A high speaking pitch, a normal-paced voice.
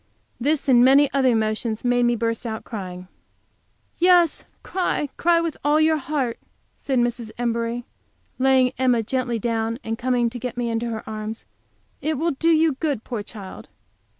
Yes: high, 245 Hz; average, 165 wpm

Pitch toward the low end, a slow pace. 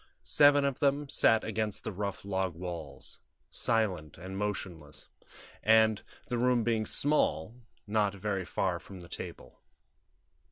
Yes: low, 105 Hz; slow, 130 wpm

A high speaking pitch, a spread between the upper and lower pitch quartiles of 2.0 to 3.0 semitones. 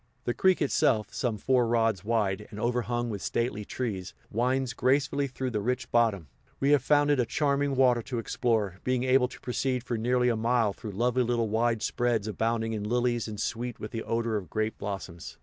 No: low, 120 Hz; narrow, 2.6 semitones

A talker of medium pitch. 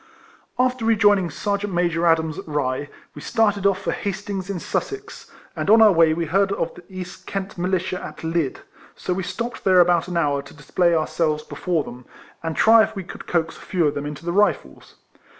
Yes: medium, 180 Hz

